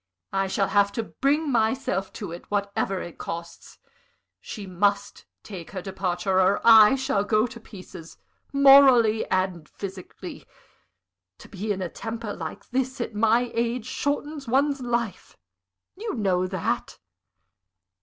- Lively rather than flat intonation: No, average, 4.4 semitones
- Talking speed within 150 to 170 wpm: No, slow, 135 wpm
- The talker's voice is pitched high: Yes, high, 210 Hz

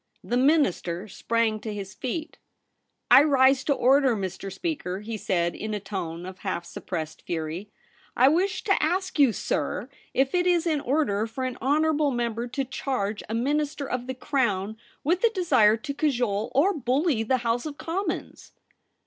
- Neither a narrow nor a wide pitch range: No, wide, 6.2 semitones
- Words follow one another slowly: No, average, 190 wpm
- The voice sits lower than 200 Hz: No, very high, 255 Hz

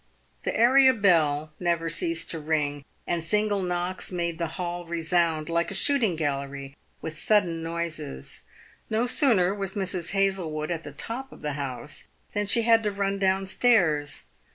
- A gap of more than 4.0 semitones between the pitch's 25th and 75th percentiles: Yes, average, 4.5 semitones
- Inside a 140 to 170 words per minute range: Yes, average, 160 wpm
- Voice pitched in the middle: Yes, medium, 175 Hz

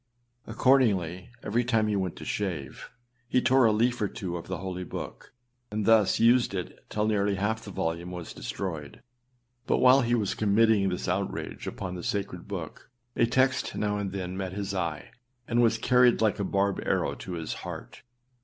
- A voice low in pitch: Yes, low, 100 Hz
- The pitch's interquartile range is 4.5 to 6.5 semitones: No, average, 3.7 semitones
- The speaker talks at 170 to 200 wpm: Yes, average, 185 wpm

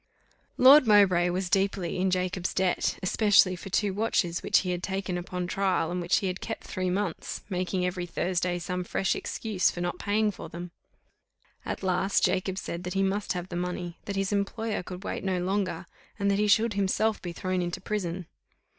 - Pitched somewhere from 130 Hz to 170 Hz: No, medium, 185 Hz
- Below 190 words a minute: No, average, 195 wpm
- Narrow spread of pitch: Yes, narrow, 1.9 semitones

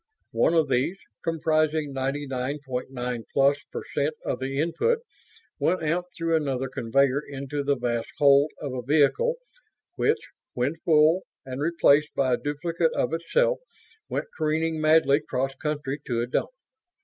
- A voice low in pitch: No, medium, 145 Hz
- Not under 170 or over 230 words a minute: No, average, 150 wpm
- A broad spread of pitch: No, average, 3.2 semitones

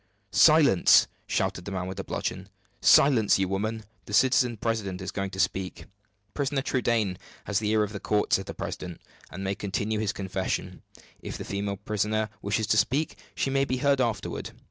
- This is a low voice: Yes, low, 105 Hz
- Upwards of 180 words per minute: Yes, average, 190 wpm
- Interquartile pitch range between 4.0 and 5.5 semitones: No, average, 3.3 semitones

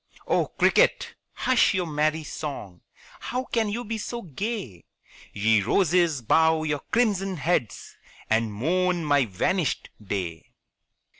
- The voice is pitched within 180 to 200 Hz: No, medium, 160 Hz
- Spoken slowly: Yes, slow, 125 wpm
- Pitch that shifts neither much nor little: No, wide, 9.0 semitones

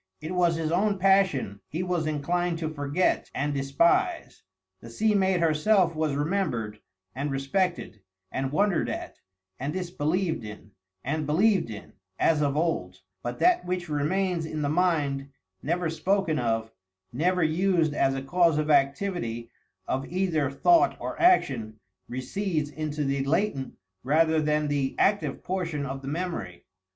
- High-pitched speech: No, medium, 155 Hz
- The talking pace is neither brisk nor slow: Yes, average, 145 wpm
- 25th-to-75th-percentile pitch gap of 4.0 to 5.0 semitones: Yes, average, 4.6 semitones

